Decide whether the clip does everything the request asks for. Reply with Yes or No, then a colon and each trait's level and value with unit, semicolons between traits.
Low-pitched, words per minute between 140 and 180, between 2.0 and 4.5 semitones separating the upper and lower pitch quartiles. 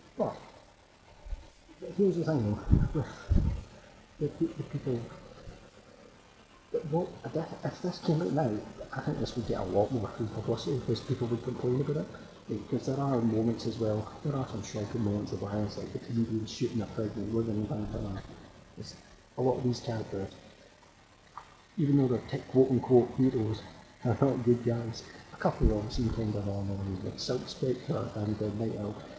Yes: low, 115 Hz; average, 165 wpm; average, 3.7 semitones